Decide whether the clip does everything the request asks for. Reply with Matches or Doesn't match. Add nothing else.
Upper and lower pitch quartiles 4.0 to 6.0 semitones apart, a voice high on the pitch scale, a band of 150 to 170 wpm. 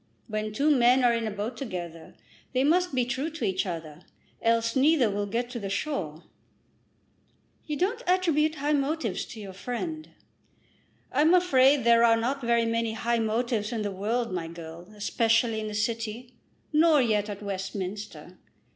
Matches